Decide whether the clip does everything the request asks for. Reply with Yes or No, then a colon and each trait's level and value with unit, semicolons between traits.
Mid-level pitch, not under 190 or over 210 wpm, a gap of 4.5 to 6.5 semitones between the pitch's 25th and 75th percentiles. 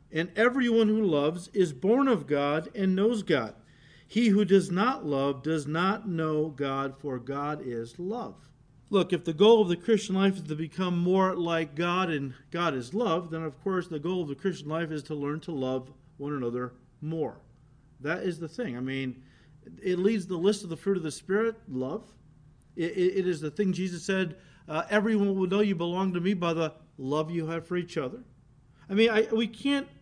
Yes: medium, 165 Hz; fast, 205 wpm; average, 4.9 semitones